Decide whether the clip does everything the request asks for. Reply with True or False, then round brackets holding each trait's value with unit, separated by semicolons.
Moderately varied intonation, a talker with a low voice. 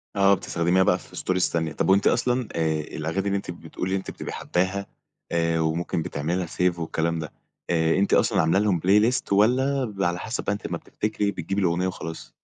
True (3.2 semitones; 90 Hz)